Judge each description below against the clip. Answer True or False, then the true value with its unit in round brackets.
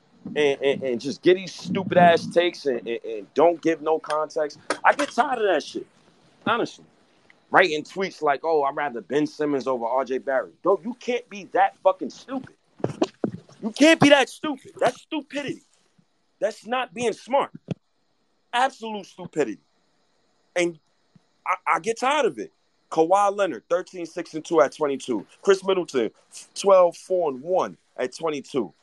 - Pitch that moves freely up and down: True (7.6 semitones)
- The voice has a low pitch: False (185 Hz)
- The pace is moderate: True (160 wpm)